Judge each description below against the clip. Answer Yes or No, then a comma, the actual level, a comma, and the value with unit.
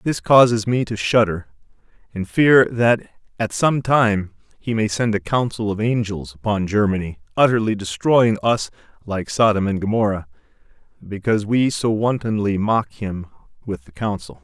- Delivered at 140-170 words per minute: Yes, average, 150 wpm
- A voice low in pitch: Yes, low, 105 Hz